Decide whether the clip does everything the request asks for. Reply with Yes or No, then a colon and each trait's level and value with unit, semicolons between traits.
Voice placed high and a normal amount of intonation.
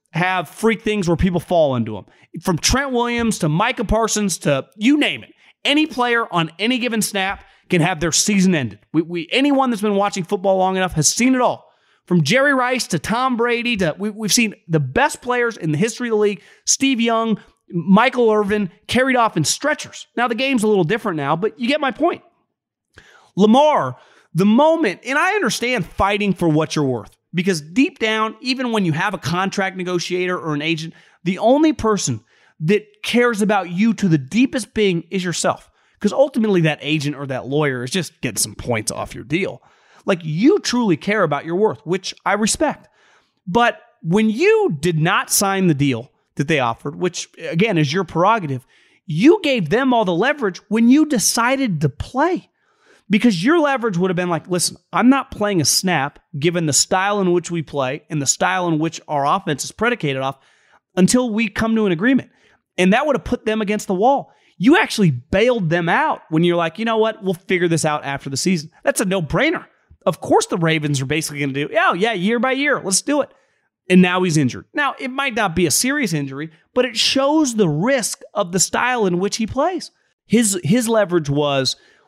No: high, 195 Hz; wide, 6.0 semitones